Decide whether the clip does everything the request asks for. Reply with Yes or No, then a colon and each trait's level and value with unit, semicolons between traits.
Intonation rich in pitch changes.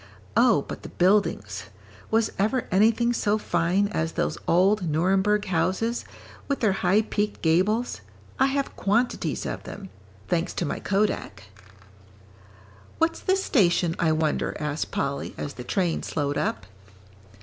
No: average, 5.0 semitones